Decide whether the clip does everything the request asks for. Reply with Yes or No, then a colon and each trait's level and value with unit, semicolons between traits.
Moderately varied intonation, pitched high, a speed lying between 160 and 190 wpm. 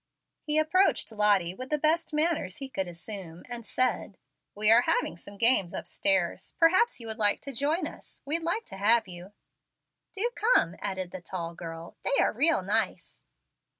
No: wide, 8.2 semitones; high, 225 Hz; average, 175 wpm